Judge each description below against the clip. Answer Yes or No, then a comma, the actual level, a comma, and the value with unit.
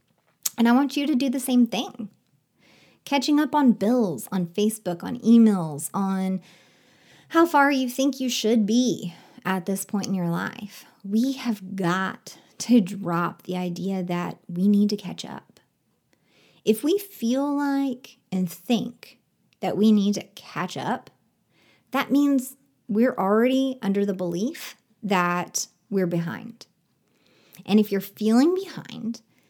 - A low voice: No, high, 215 Hz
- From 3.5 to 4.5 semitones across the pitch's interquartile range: No, average, 5.1 semitones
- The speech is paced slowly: No, average, 145 wpm